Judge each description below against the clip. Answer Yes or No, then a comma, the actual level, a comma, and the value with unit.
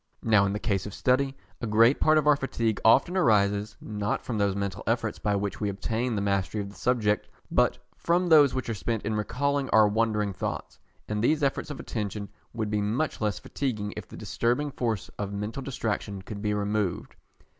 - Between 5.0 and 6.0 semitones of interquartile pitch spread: No, average, 3.7 semitones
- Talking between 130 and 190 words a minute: No, average, 200 wpm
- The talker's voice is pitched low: Yes, low, 110 Hz